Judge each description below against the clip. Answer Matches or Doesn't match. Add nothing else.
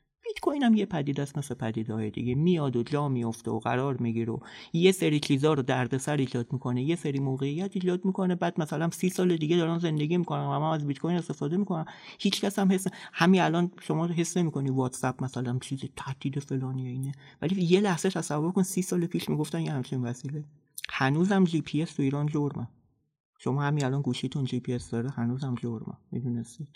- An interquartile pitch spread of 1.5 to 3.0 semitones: Doesn't match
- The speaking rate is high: Matches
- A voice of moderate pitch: Matches